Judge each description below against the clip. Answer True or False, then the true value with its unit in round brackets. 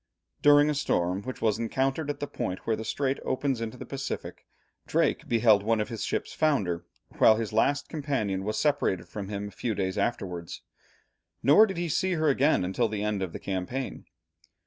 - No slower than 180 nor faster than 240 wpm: True (190 wpm)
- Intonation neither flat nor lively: False (5.9 semitones)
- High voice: False (115 Hz)